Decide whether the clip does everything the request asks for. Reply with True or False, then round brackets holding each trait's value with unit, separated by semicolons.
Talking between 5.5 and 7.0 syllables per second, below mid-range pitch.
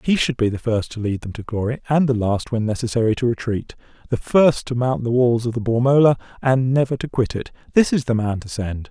True (5.7 syllables/s; 120 Hz)